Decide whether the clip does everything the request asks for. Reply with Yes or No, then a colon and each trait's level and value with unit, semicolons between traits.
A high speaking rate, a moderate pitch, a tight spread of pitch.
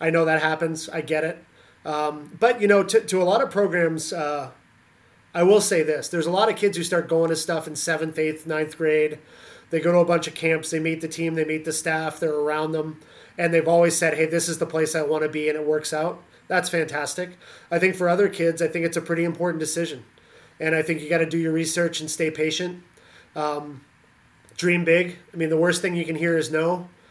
Yes: fast, 245 wpm; medium, 165 Hz; narrow, 1.6 semitones